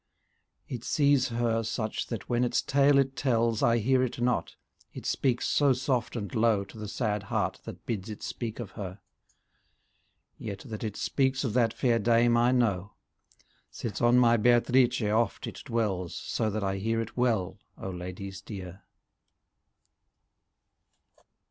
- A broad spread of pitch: No, average, 3.0 semitones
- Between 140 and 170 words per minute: Yes, average, 155 wpm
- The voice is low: Yes, low, 115 Hz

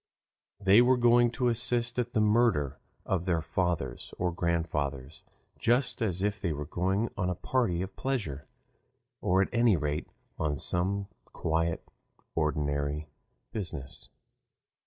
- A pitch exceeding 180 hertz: No, very low, 90 Hz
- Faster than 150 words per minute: No, slow, 135 wpm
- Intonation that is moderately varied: No, wide, 7.1 semitones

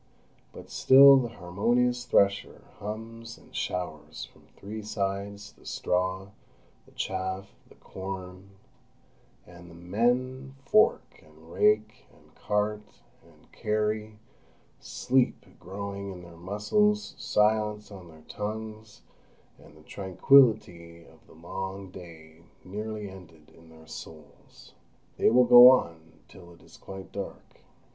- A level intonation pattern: No, average, 3.7 semitones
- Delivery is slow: Yes, slow, 120 wpm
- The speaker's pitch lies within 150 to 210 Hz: No, low, 100 Hz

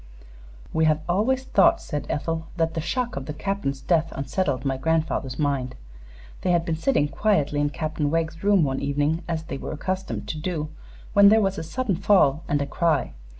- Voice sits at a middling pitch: Yes, medium, 160 Hz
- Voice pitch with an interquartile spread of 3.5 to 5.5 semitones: Yes, average, 4.4 semitones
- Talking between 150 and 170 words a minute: No, average, 195 wpm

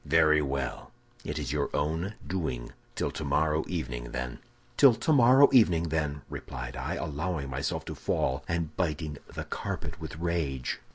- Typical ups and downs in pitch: Yes, average, 3.5 semitones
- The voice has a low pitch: Yes, very low, 75 Hz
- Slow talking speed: No, average, 150 wpm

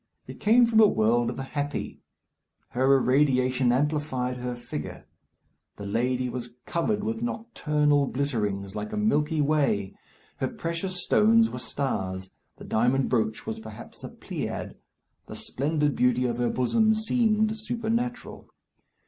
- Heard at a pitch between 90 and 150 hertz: Yes, medium, 140 Hz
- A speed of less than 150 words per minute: Yes, average, 140 wpm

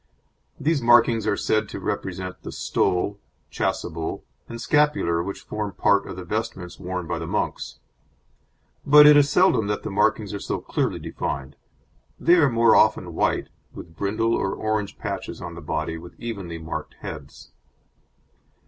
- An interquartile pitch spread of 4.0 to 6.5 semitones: Yes, average, 5.0 semitones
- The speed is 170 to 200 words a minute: No, average, 155 wpm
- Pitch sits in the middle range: No, low, 100 Hz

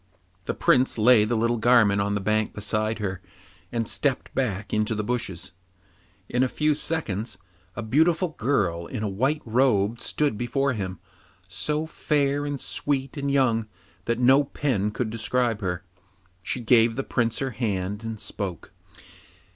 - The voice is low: Yes, low, 115 Hz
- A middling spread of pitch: Yes, average, 4.3 semitones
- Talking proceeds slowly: No, average, 155 wpm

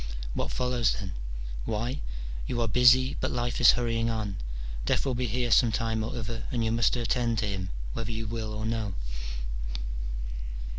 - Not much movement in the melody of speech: Yes, narrow, 1.9 semitones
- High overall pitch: No, low, 115 Hz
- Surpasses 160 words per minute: Yes, average, 170 wpm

